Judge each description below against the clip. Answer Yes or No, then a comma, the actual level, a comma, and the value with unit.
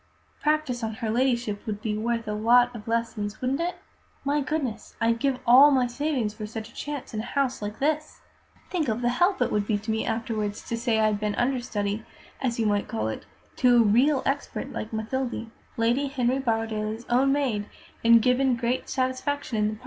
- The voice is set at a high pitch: Yes, high, 235 Hz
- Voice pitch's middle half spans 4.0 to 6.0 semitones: No, average, 3.3 semitones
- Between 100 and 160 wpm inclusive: No, average, 200 wpm